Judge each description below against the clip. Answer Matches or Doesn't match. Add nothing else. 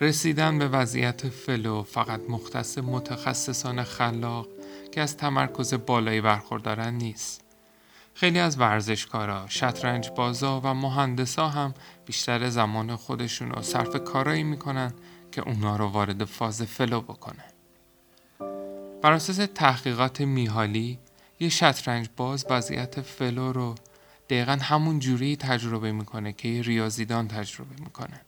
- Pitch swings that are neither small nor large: Matches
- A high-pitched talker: Doesn't match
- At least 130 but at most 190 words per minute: Doesn't match